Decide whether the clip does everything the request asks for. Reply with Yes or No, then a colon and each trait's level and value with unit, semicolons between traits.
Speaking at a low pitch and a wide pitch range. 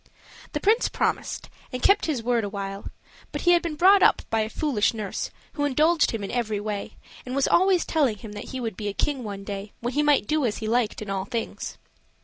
No: high, 240 Hz; wide, 6.2 semitones